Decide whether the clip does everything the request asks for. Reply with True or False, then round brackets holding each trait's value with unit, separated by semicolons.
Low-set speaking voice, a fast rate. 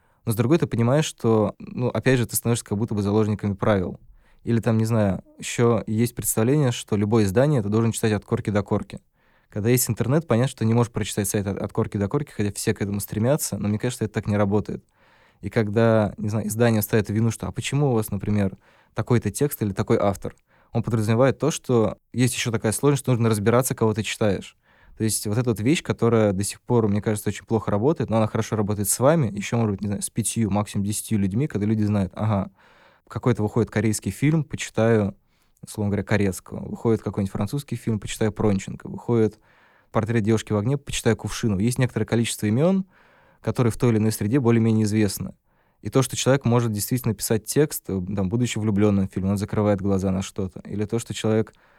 True (110 Hz; 210 wpm)